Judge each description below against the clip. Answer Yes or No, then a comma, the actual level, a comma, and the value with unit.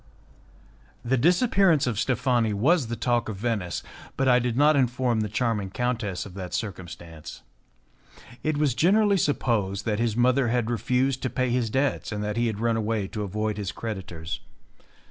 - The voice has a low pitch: Yes, low, 115 Hz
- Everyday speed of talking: Yes, average, 170 wpm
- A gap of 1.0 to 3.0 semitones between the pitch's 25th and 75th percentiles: No, average, 3.7 semitones